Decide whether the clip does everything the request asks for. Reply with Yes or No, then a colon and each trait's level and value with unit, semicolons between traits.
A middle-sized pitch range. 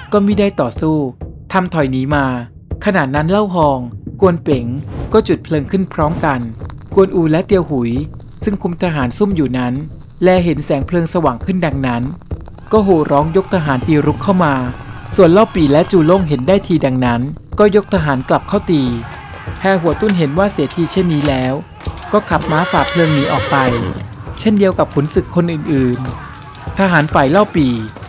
No: wide, 5.9 semitones